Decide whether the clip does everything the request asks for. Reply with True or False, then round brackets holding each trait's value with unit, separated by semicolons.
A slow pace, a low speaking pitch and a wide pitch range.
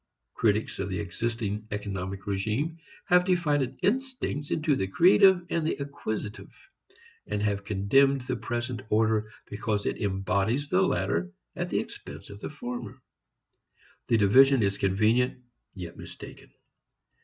True (130 wpm; 110 Hz; 5.8 semitones)